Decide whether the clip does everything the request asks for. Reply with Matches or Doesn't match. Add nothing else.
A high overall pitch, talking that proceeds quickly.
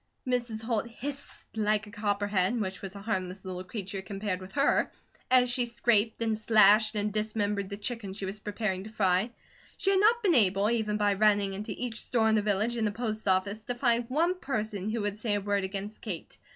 Matches